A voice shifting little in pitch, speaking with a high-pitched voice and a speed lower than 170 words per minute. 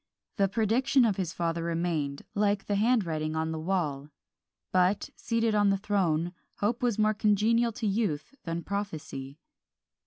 No: average, 4.5 semitones; high, 195 Hz; average, 150 wpm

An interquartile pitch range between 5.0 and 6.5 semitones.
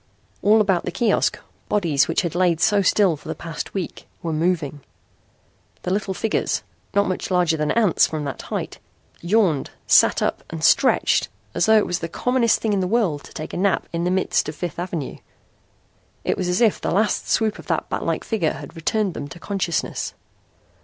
No: average, 4.0 semitones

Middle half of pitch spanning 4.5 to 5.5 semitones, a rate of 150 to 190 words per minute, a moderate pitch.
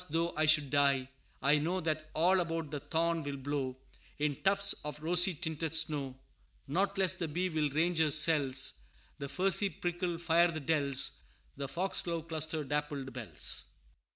No: average, 3.0 semitones; average, 160 wpm; medium, 155 Hz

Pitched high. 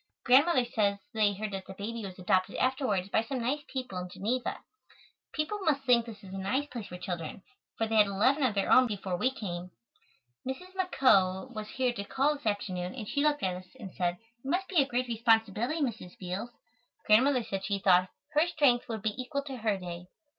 Yes: high, 225 Hz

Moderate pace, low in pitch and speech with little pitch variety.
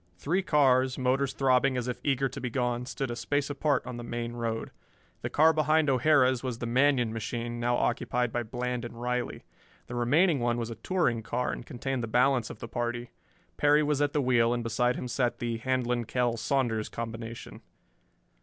Yes: average, 195 wpm; low, 125 Hz; narrow, 2.3 semitones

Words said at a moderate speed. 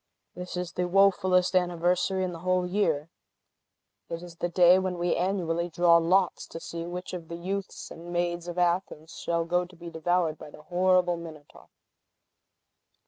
Yes: average, 170 wpm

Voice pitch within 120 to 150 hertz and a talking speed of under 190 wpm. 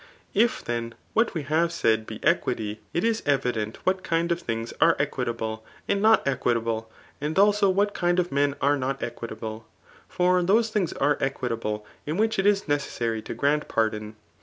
Yes: medium, 140 Hz; average, 180 wpm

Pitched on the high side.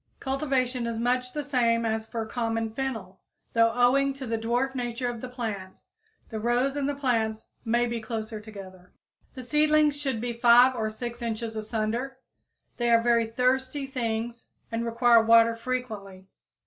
Yes: high, 235 Hz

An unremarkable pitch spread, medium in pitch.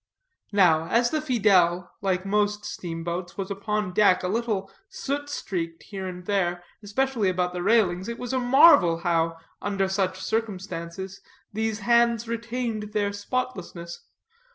No: average, 4.1 semitones; high, 200 Hz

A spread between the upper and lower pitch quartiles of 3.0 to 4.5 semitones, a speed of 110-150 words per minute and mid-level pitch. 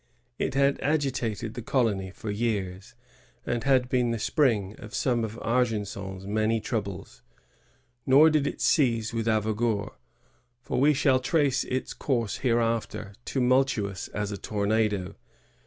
No: average, 3.8 semitones; average, 140 wpm; low, 115 Hz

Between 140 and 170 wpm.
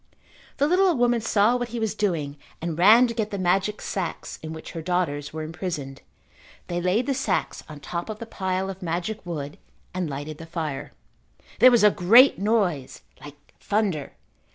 No: average, 185 wpm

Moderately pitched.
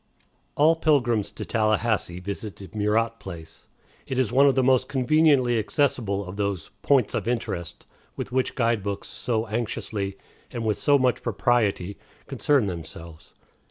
No: low, 115 Hz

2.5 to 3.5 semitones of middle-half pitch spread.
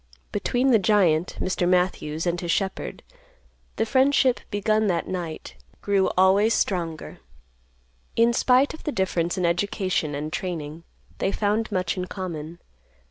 No: average, 4.0 semitones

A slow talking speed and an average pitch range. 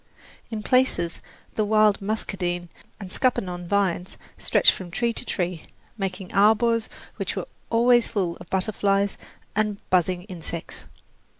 Yes: slow, 125 wpm; average, 3.3 semitones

